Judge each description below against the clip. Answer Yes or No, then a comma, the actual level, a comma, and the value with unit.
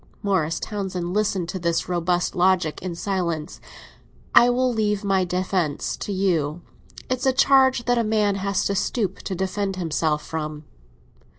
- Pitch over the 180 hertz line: Yes, high, 190 Hz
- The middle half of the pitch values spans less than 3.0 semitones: No, average, 3.4 semitones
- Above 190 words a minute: No, average, 155 wpm